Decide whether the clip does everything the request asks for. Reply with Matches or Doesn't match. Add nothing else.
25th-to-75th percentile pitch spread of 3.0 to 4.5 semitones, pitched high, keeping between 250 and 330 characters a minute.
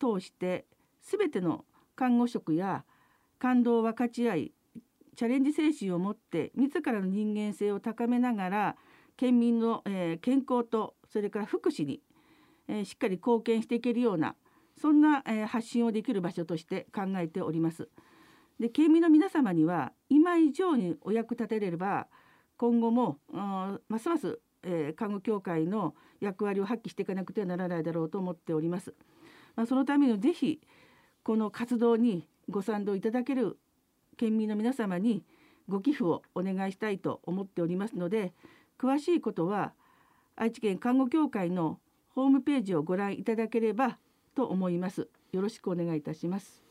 Doesn't match